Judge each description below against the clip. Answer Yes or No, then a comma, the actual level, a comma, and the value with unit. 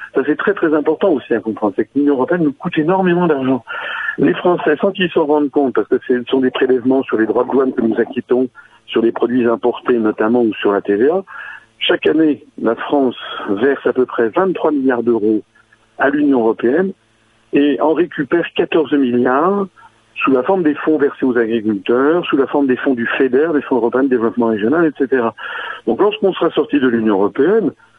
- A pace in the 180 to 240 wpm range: Yes, average, 200 wpm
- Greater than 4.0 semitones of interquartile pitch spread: Yes, average, 4.6 semitones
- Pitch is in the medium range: No, low, 130 Hz